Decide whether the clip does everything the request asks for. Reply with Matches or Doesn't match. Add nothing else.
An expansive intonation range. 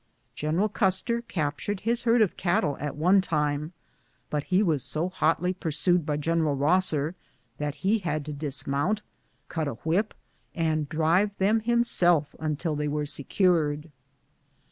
Doesn't match